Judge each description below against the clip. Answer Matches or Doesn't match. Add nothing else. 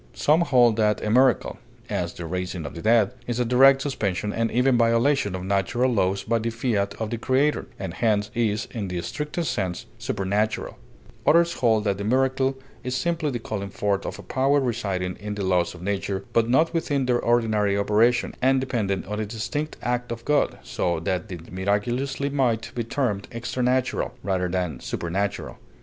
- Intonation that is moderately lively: Matches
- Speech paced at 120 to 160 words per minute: Doesn't match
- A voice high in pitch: Doesn't match